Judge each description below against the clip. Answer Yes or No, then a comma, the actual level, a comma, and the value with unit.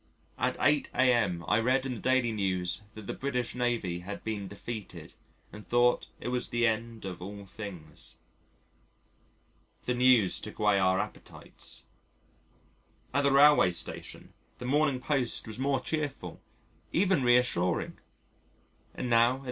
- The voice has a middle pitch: No, low, 120 Hz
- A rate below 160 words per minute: Yes, average, 145 wpm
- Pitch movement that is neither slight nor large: Yes, average, 4.2 semitones